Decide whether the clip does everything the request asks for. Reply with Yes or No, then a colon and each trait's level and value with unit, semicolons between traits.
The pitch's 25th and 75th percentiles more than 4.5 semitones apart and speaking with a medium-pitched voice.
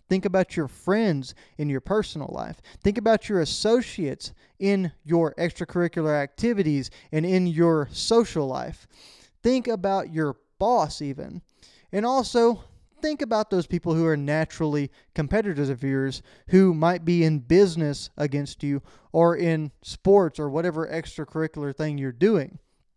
Yes: average, 4.9 semitones; medium, 165 Hz